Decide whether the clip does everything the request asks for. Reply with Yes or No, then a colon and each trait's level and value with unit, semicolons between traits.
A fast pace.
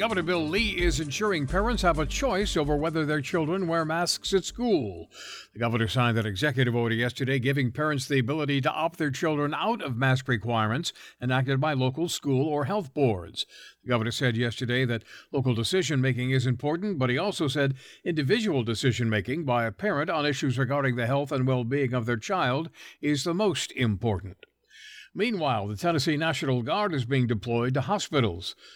No: average, 185 wpm